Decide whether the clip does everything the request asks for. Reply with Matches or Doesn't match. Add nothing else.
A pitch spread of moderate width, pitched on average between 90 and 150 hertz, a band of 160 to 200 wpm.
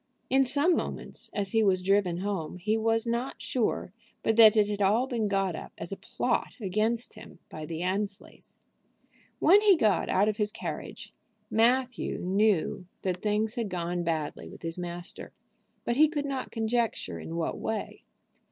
Doesn't match